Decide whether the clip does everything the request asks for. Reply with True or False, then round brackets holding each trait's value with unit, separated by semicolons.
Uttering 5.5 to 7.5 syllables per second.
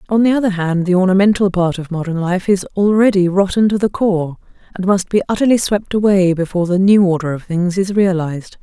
True (5.8 syllables/s)